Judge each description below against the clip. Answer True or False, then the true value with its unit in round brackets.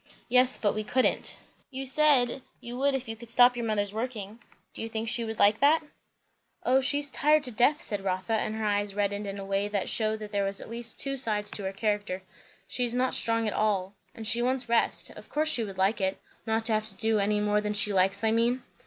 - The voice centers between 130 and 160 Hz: False (220 Hz)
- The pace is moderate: False (240 wpm)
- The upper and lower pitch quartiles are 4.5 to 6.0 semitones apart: False (3.2 semitones)